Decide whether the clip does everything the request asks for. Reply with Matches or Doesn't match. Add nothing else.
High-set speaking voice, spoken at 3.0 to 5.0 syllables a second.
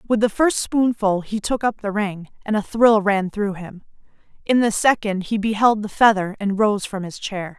Matches